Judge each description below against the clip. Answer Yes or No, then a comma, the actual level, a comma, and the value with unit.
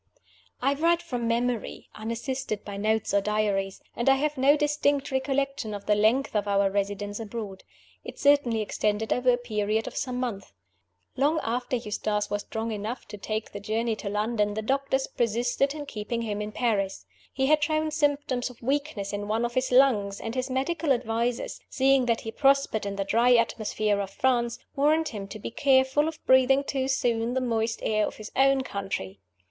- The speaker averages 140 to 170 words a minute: No, average, 185 wpm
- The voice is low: No, high, 235 Hz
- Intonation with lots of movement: No, average, 4.2 semitones